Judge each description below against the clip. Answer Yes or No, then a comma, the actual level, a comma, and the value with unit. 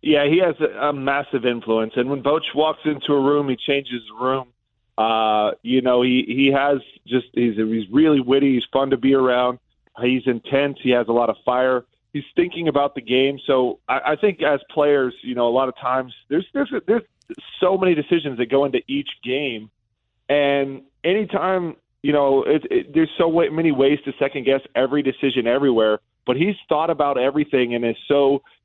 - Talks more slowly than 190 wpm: No, average, 195 wpm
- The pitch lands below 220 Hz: Yes, low, 135 Hz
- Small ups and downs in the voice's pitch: No, average, 3.0 semitones